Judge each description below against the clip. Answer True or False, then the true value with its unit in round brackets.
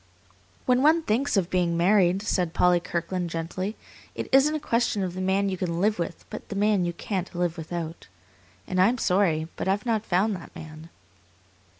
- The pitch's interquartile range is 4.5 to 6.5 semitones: False (3.4 semitones)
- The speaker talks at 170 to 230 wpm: True (195 wpm)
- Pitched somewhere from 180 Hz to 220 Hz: True (185 Hz)